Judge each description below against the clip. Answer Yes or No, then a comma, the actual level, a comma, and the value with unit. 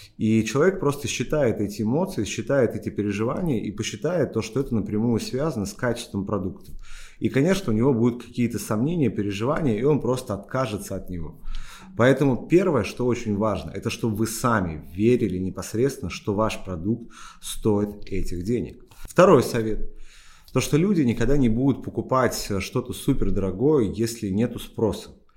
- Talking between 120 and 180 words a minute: Yes, average, 155 wpm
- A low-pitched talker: Yes, low, 110 Hz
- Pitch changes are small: No, average, 3.8 semitones